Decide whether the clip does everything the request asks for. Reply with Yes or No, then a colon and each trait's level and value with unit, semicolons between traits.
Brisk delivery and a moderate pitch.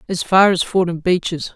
No: average, 190 wpm; medium, 175 Hz